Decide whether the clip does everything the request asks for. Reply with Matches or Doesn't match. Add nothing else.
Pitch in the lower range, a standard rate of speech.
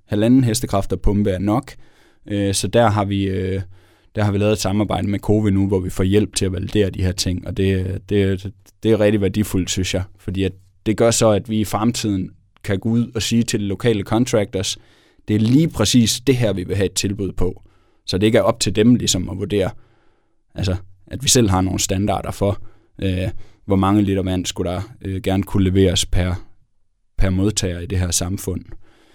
Matches